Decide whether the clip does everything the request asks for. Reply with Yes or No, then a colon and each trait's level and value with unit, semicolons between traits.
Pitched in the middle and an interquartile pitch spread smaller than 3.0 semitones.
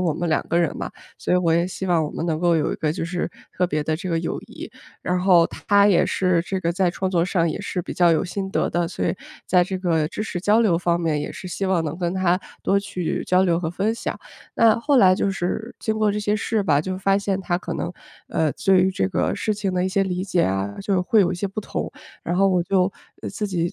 Yes: medium, 180 Hz; narrow, 2.5 semitones